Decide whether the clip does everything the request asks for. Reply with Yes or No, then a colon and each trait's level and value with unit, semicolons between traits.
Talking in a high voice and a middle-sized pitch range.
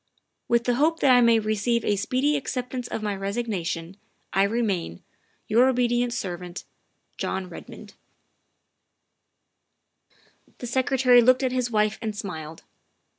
Yes: high, 235 Hz; average, 4.1 semitones